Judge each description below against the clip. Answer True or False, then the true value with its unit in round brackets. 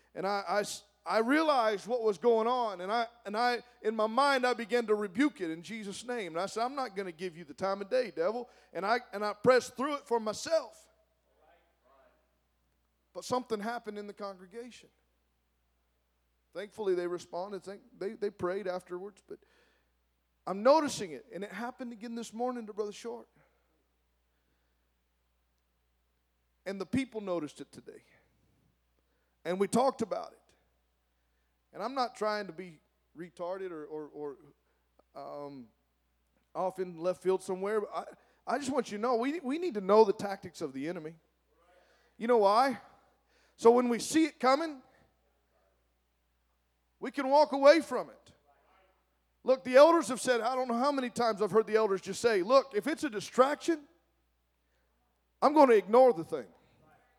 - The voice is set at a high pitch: True (205 Hz)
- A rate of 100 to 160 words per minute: False (170 wpm)